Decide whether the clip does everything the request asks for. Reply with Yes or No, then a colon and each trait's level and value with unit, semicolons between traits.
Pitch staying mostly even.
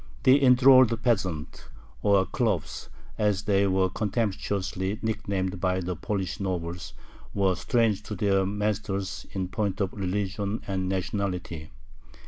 Yes: narrow, 2.1 semitones